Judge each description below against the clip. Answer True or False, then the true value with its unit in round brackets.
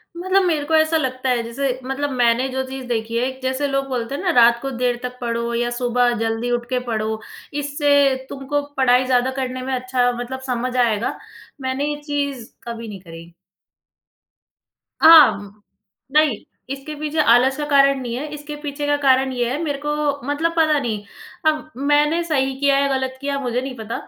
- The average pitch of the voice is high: True (260 Hz)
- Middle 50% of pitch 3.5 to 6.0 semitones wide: False (3.1 semitones)